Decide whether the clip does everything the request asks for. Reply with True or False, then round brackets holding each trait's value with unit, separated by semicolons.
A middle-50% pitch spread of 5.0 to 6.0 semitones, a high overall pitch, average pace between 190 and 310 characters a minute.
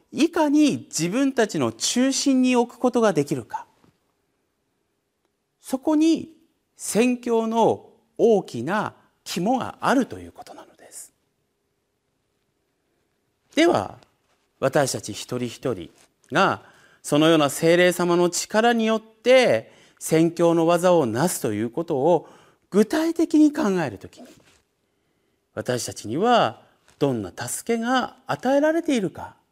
False (8.6 semitones; 230 Hz; 220 characters per minute)